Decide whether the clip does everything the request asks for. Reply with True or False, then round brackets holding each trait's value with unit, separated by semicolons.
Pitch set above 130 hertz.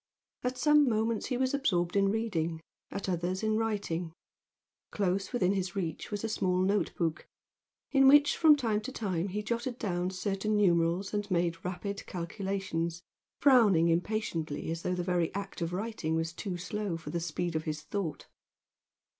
True (190 Hz)